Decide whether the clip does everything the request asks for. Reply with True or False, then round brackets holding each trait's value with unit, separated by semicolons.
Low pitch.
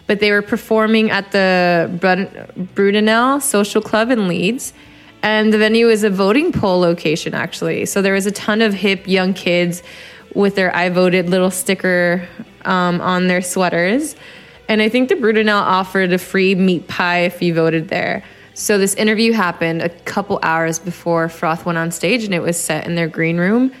False (190 Hz)